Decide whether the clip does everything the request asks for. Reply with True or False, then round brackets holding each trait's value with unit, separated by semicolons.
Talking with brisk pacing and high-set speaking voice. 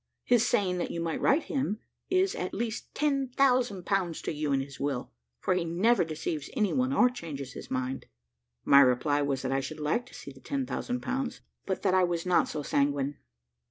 False (215 wpm; 175 Hz)